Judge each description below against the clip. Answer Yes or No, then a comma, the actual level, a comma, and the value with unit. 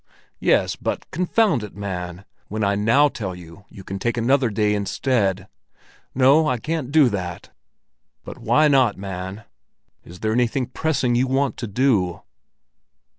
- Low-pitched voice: Yes, low, 110 Hz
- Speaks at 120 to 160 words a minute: Yes, average, 150 wpm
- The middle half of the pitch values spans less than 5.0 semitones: No, wide, 5.5 semitones